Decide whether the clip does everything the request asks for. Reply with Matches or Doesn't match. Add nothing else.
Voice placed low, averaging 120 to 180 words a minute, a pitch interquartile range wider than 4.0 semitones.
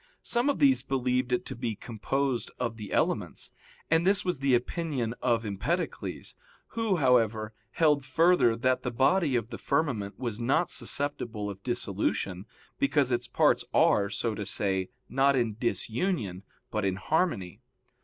Matches